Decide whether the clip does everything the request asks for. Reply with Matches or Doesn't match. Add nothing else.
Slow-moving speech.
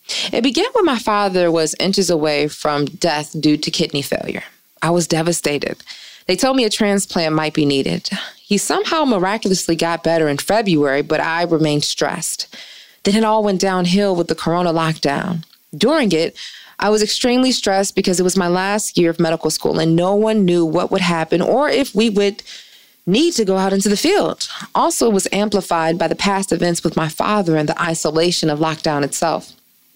Doesn't match